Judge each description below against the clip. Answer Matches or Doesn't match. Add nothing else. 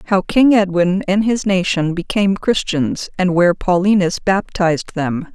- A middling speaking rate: Matches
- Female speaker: Matches